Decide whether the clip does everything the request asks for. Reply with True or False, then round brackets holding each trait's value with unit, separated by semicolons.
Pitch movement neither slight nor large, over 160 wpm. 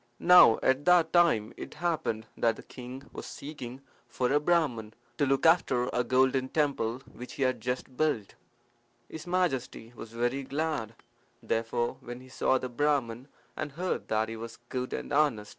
True (4.0 semitones; 175 wpm)